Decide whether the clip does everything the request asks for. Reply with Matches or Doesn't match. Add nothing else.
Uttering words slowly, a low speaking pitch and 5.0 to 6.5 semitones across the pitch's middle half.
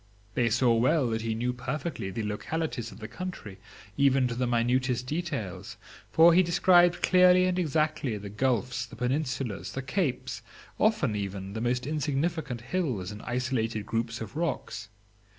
Doesn't match